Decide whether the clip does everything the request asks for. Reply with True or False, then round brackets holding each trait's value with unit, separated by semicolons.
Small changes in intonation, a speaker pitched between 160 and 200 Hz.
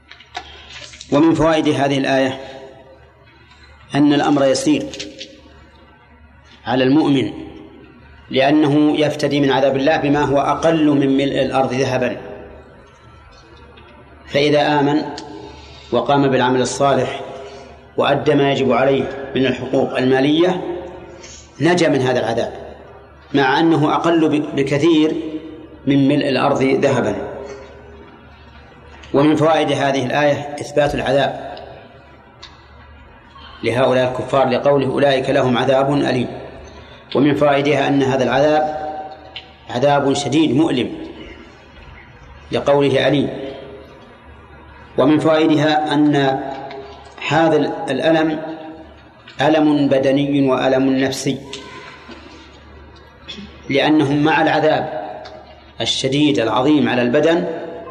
False (2.3 semitones; 140 Hz)